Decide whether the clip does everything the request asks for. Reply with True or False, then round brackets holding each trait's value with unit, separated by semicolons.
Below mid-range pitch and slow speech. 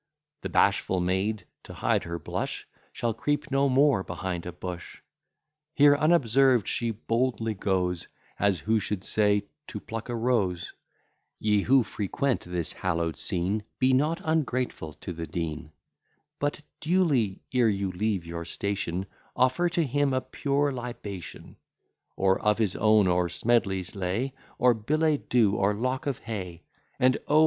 False (110 Hz; 150 wpm)